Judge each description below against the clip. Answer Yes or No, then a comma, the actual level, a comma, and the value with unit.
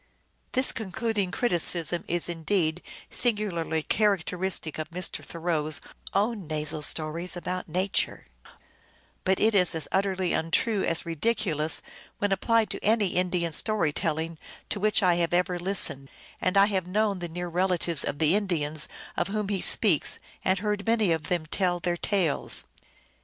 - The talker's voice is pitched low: No, medium, 180 Hz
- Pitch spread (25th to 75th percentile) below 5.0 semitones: Yes, average, 3.5 semitones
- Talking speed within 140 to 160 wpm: Yes, average, 150 wpm